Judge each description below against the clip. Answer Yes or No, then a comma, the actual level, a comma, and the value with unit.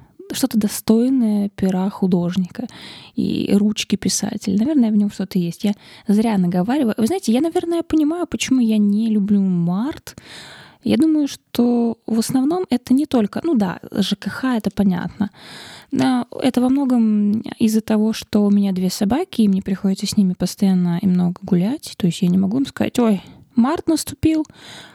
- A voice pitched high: Yes, high, 215 Hz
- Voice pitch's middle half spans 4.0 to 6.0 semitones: Yes, average, 4.3 semitones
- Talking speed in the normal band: No, fast, 165 wpm